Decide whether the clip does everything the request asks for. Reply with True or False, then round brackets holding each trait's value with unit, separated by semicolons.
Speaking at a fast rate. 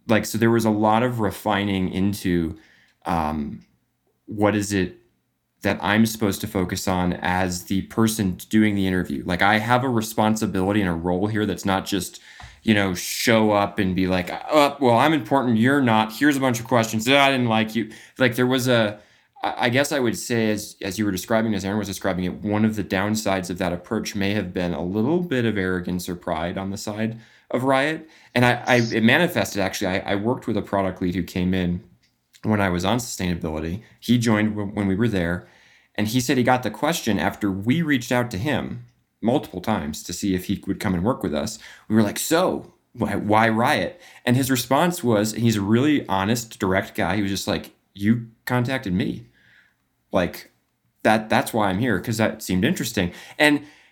True (215 wpm)